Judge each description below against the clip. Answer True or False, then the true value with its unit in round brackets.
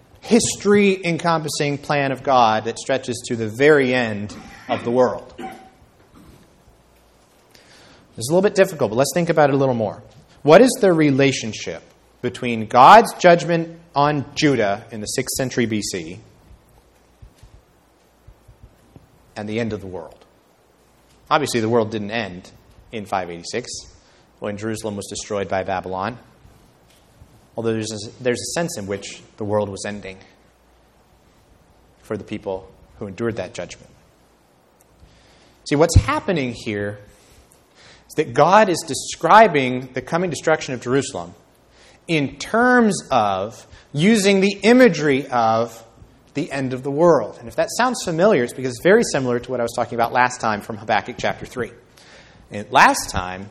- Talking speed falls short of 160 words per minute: True (145 wpm)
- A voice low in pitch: True (125 Hz)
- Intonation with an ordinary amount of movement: False (6.2 semitones)